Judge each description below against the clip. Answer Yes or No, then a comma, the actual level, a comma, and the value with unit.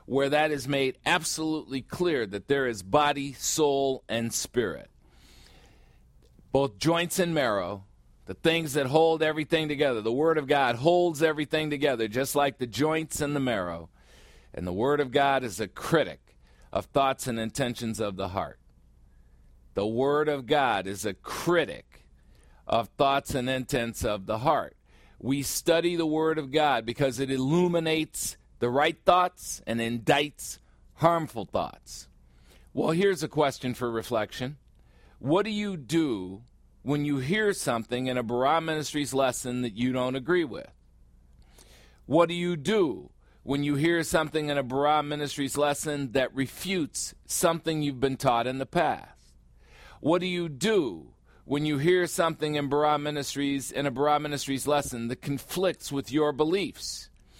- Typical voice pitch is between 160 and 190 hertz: No, medium, 140 Hz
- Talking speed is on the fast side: No, average, 155 wpm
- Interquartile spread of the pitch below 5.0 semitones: No, average, 5.3 semitones